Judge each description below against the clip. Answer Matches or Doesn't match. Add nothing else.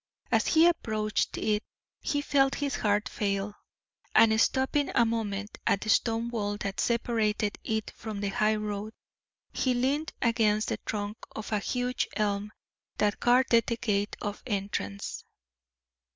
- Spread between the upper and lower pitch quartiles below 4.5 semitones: Matches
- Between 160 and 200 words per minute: Doesn't match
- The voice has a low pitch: Doesn't match